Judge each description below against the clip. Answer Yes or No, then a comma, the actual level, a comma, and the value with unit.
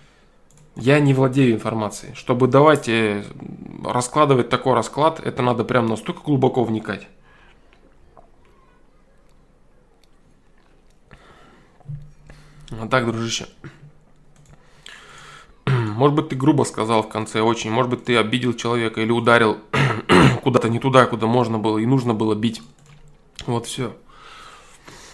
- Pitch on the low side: Yes, low, 125 Hz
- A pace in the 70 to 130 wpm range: Yes, slow, 110 wpm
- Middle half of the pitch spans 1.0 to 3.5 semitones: No, average, 4.1 semitones